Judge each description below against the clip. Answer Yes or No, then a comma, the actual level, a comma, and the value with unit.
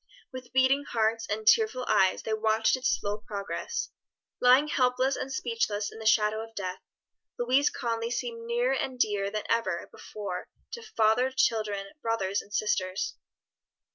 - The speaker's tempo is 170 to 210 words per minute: No, average, 150 wpm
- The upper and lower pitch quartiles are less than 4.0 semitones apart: Yes, average, 3.2 semitones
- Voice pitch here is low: No, high, 225 Hz